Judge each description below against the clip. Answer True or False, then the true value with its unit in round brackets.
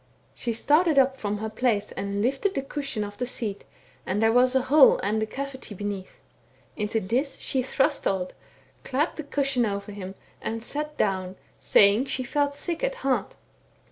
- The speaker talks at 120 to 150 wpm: False (180 wpm)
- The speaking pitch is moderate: False (245 Hz)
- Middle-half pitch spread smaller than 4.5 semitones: False (5.2 semitones)